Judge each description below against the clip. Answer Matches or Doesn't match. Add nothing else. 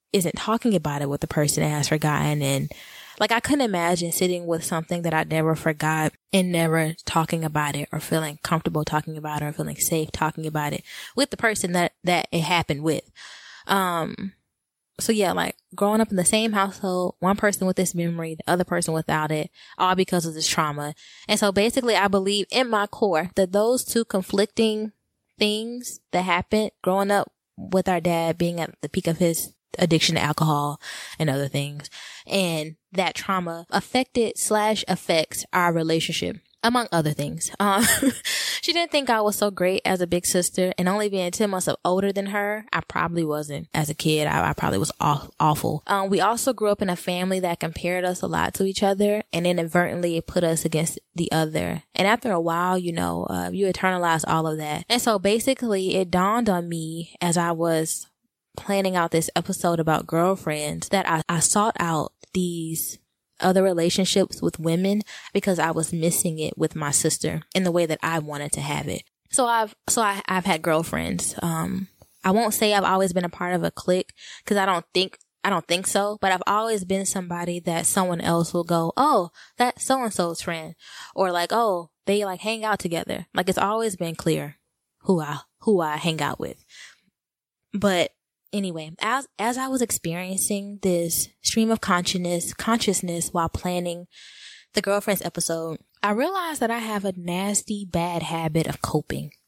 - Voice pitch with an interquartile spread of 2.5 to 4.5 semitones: Matches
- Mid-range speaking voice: Matches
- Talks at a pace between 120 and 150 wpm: Doesn't match